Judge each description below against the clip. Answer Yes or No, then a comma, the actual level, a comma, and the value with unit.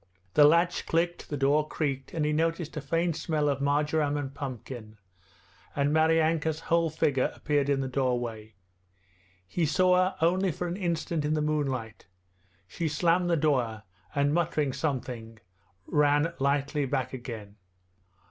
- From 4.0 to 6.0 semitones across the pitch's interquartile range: No, average, 3.4 semitones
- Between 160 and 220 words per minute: No, average, 145 wpm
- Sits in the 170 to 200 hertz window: No, medium, 150 Hz